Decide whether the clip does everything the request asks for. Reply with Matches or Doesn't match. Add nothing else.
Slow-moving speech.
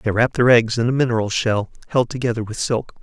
Doesn't match